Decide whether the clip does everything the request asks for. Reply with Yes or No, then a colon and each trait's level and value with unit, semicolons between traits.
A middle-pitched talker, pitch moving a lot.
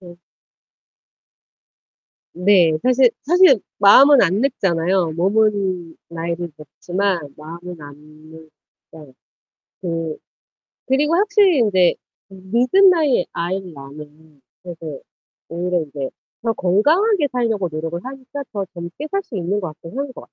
Yes: medium, 180 Hz; wide, 7.2 semitones